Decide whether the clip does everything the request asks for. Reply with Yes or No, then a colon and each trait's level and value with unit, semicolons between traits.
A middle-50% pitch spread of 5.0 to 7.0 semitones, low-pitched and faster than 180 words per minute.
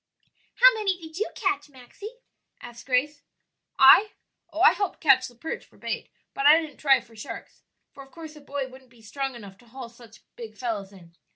No: average, 5.3 semitones; very high, 270 Hz; average, 200 wpm